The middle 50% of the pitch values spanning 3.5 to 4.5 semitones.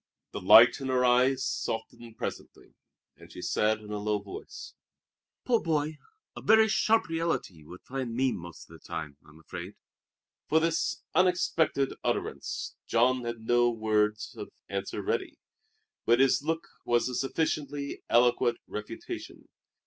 No: average, 5.2 semitones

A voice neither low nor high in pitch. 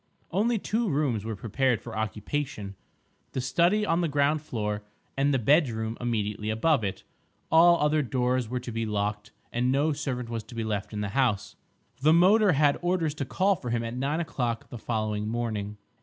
No: low, 125 Hz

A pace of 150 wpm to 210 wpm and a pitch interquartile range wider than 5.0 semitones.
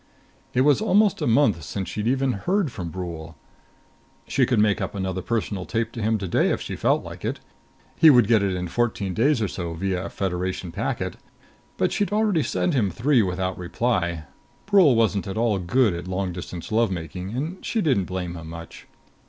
Yes: average, 195 wpm; wide, 5.6 semitones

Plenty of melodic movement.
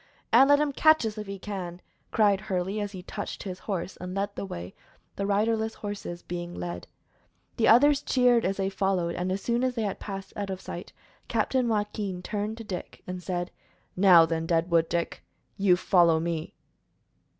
No: average, 3.3 semitones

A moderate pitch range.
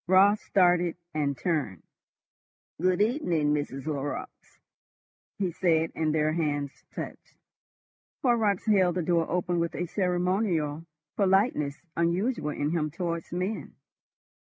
Yes: average, 3.6 semitones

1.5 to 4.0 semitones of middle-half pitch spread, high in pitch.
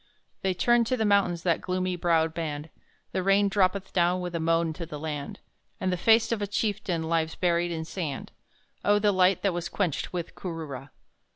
No: average, 3.2 semitones; medium, 180 Hz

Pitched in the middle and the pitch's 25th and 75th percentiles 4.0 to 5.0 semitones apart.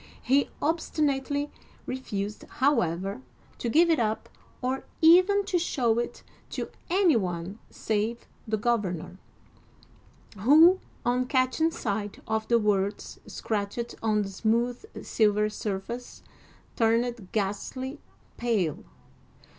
No: high, 235 Hz; average, 4.7 semitones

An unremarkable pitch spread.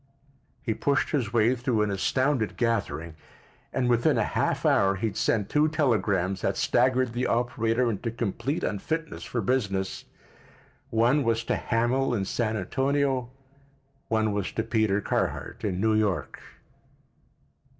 Yes: average, 3.6 semitones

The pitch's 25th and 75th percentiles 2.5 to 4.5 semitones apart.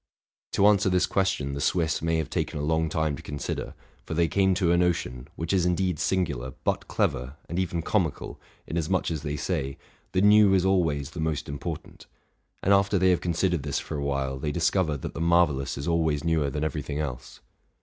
Yes: average, 4.0 semitones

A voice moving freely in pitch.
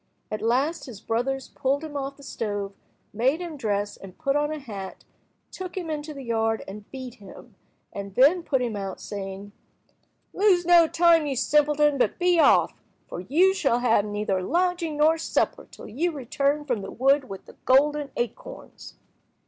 Yes: wide, 6.1 semitones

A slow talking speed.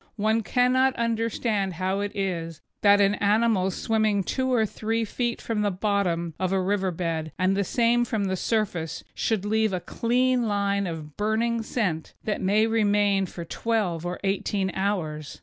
No: average, 165 wpm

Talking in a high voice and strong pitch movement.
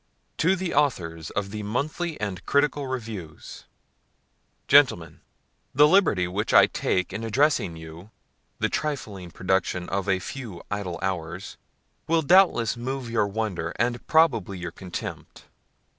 No: low, 105 Hz; wide, 7.5 semitones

